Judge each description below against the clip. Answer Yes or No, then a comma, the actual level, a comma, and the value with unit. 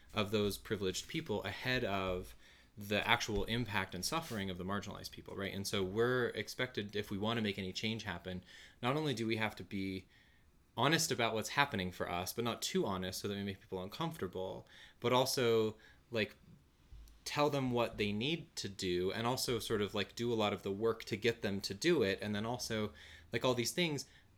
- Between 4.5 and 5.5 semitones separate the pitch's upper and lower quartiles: No, average, 3.8 semitones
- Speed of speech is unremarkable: No, fast, 210 wpm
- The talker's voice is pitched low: Yes, low, 105 Hz